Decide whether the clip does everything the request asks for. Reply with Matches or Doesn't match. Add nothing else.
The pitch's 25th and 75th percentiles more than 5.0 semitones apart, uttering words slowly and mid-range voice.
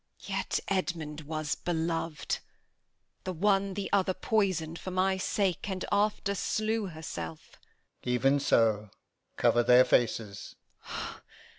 Matches